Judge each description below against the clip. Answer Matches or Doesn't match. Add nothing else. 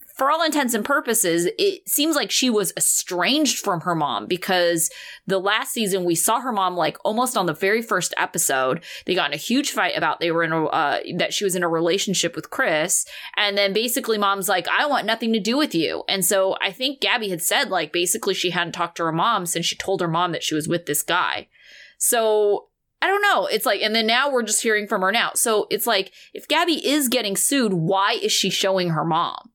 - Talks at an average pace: Doesn't match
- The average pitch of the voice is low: Doesn't match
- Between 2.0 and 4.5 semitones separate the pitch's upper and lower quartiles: Doesn't match